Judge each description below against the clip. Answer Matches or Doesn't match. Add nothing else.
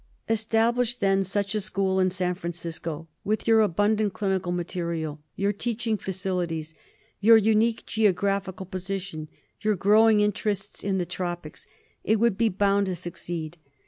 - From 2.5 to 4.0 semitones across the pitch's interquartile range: Matches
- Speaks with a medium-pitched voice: Doesn't match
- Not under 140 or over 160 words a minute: Matches